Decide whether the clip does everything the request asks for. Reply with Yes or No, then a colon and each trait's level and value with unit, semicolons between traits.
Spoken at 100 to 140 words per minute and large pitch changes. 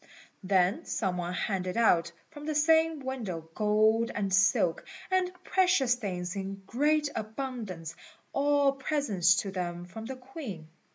Yes: slow, 135 wpm; wide, 7.1 semitones